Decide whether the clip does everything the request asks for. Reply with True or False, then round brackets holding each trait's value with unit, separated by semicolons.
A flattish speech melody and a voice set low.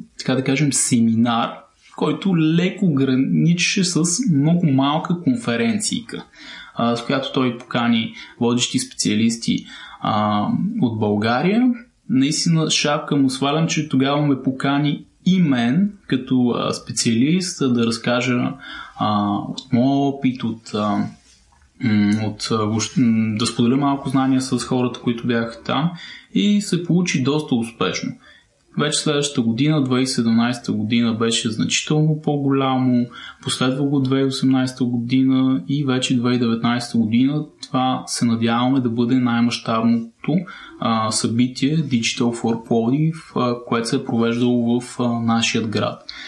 False (3.5 semitones; 130 Hz)